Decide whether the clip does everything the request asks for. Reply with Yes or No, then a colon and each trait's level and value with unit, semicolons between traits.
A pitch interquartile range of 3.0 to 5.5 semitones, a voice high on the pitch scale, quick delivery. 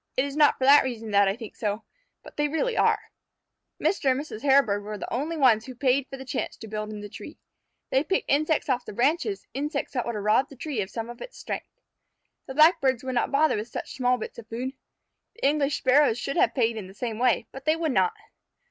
Yes: average, 4.4 semitones; very high, 260 Hz; fast, 240 wpm